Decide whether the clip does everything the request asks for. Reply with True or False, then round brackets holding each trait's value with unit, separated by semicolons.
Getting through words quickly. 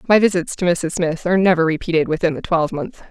True (210 wpm)